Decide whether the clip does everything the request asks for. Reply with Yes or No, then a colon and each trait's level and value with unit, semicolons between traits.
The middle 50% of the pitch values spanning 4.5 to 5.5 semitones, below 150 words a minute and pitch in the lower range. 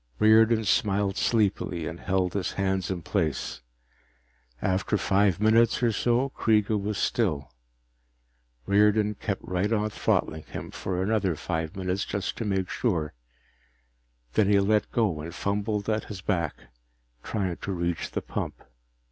No: average, 2.8 semitones; average, 140 wpm; low, 100 Hz